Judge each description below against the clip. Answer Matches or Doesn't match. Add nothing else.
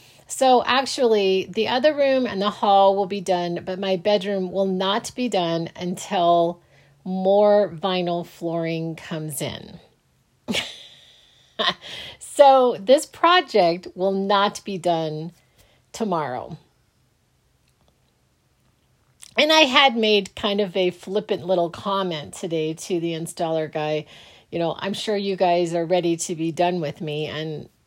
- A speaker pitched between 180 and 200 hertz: Matches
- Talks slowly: Matches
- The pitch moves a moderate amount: Matches